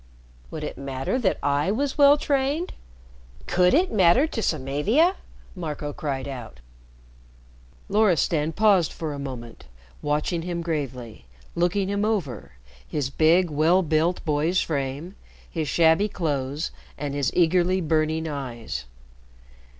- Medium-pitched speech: Yes, medium, 160 Hz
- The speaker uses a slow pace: Yes, slow, 125 wpm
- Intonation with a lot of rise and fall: No, average, 4.9 semitones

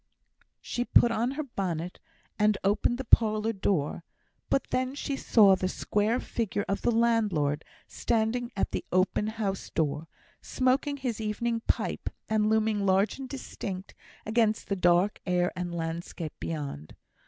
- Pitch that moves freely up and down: No, average, 4.4 semitones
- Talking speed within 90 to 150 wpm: Yes, average, 145 wpm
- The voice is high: Yes, high, 210 Hz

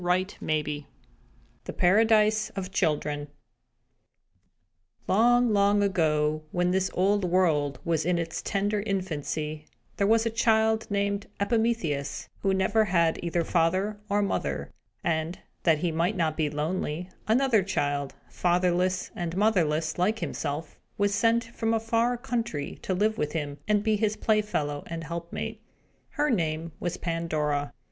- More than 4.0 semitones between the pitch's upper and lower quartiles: Yes, average, 5.0 semitones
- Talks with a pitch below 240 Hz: Yes, medium, 185 Hz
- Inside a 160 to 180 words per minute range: No, average, 140 wpm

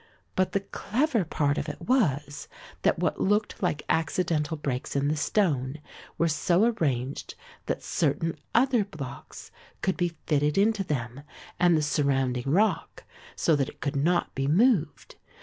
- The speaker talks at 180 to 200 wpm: No, average, 150 wpm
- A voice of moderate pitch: Yes, medium, 160 Hz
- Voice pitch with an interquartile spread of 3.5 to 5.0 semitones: No, wide, 5.5 semitones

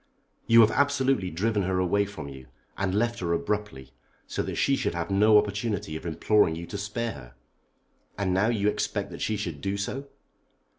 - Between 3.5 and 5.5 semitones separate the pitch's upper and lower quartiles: Yes, average, 4.1 semitones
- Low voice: Yes, low, 100 Hz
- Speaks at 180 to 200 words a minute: Yes, average, 190 wpm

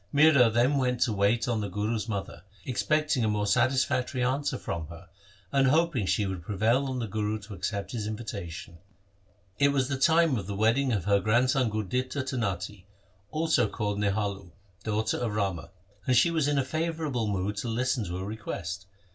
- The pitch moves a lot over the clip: No, average, 4.5 semitones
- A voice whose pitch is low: Yes, low, 115 Hz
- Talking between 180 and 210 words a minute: Yes, average, 185 wpm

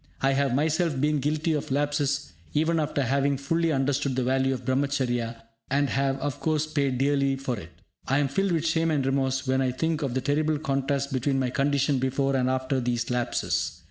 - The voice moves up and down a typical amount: No, narrow, 2.0 semitones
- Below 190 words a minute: No, average, 200 wpm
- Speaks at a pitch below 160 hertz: Yes, medium, 140 Hz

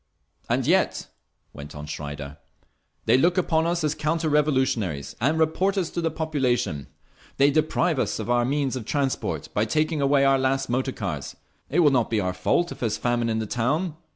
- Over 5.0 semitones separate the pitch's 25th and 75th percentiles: Yes, wide, 5.6 semitones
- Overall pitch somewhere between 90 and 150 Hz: Yes, low, 135 Hz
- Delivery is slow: No, average, 195 wpm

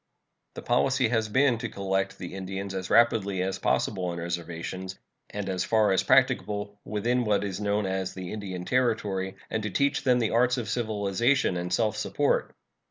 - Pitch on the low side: Yes, low, 100 Hz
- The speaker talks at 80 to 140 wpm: No, average, 175 wpm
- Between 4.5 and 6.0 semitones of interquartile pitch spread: No, average, 3.7 semitones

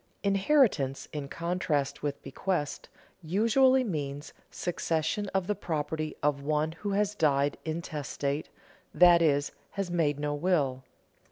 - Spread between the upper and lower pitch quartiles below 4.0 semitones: No, average, 4.8 semitones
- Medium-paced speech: No, slow, 125 wpm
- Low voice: No, medium, 160 Hz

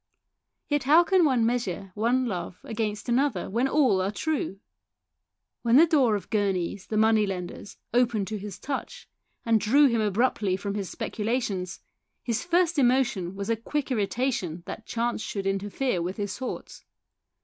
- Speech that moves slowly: No, average, 160 wpm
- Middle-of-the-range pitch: No, high, 225 Hz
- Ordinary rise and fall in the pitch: Yes, average, 4.7 semitones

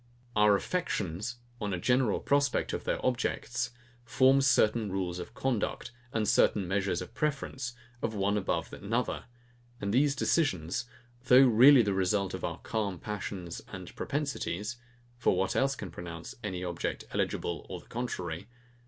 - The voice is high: No, low, 105 Hz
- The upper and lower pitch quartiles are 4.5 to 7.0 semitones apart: Yes, average, 5.1 semitones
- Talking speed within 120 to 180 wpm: Yes, average, 150 wpm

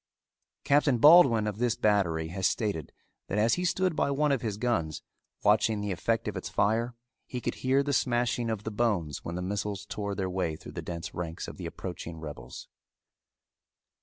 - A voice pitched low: Yes, low, 105 Hz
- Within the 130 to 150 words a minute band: No, average, 190 wpm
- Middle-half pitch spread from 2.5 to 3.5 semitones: No, average, 5.0 semitones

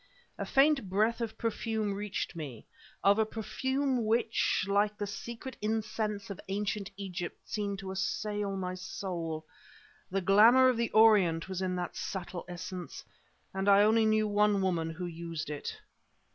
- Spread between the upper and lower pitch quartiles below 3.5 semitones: Yes, average, 3.0 semitones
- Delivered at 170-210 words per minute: No, average, 155 wpm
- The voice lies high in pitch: Yes, high, 200 Hz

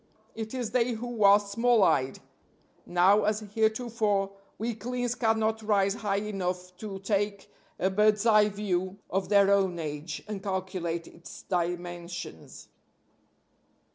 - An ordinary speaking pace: No, slow, 125 wpm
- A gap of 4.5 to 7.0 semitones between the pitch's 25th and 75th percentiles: No, average, 3.0 semitones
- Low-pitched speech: No, high, 200 Hz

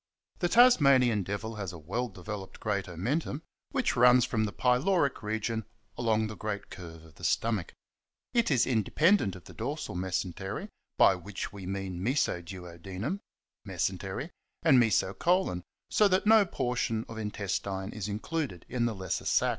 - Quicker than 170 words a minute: No, average, 155 wpm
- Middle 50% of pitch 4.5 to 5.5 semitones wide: Yes, average, 5.2 semitones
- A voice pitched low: Yes, low, 110 Hz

